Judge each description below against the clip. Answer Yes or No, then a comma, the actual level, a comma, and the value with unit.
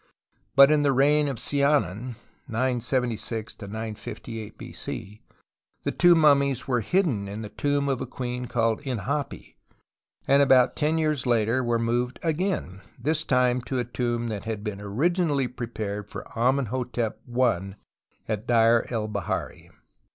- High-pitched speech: No, low, 125 Hz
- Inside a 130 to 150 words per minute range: Yes, average, 140 wpm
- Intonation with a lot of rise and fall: No, average, 3.9 semitones